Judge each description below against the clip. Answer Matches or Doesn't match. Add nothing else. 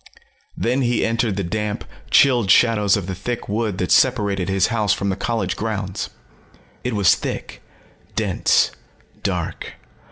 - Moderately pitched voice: Doesn't match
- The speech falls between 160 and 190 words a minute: Doesn't match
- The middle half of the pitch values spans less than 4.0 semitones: Matches